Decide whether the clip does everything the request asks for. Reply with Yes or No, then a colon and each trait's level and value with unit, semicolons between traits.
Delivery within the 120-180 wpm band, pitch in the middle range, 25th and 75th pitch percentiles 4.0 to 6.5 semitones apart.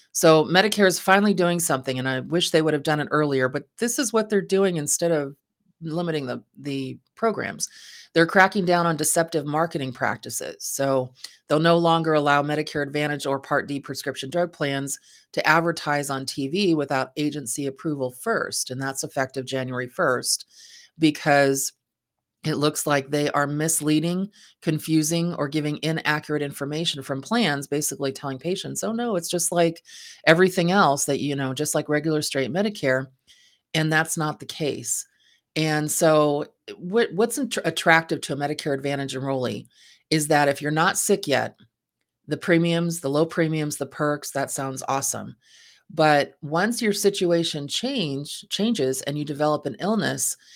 No: average, 160 wpm; medium, 150 Hz; average, 3.4 semitones